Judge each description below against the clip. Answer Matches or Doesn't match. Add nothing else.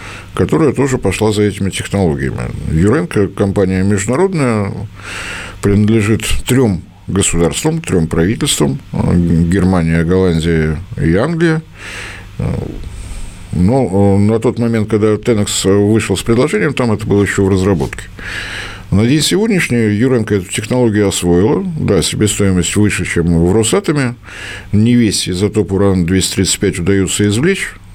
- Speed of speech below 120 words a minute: Matches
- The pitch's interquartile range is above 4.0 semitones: Doesn't match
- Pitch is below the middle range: Matches